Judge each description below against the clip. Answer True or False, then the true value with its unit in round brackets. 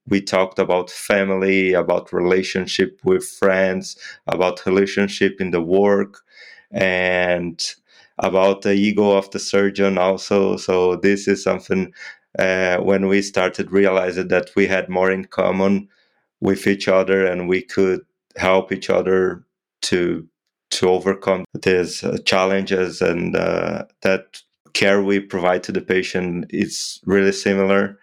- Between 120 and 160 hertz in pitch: False (95 Hz)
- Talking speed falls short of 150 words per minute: True (135 wpm)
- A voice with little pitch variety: True (1.1 semitones)